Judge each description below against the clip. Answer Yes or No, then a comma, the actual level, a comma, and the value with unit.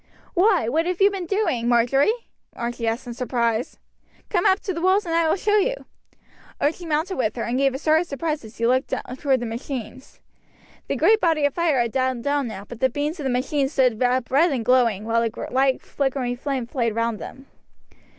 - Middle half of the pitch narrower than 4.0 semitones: No, wide, 5.4 semitones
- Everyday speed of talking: No, fast, 215 wpm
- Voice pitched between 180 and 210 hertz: No, very high, 265 Hz